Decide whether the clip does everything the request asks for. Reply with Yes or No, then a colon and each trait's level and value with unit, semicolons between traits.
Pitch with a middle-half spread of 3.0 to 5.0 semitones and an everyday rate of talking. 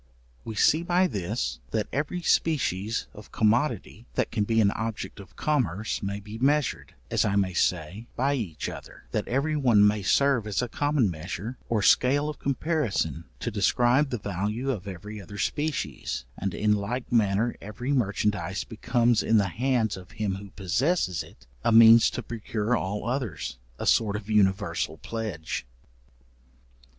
Yes: average, 4.1 semitones; average, 160 wpm